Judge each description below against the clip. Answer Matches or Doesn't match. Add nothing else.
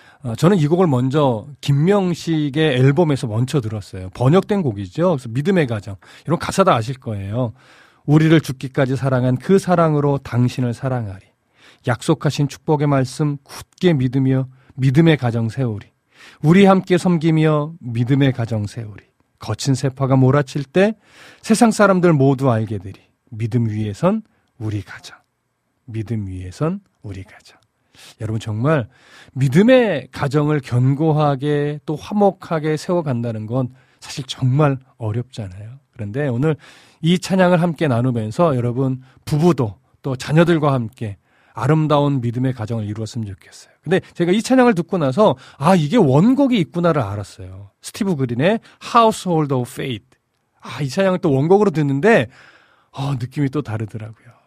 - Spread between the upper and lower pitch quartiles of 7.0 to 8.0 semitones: Doesn't match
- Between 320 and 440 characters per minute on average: Matches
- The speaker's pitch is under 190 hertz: Matches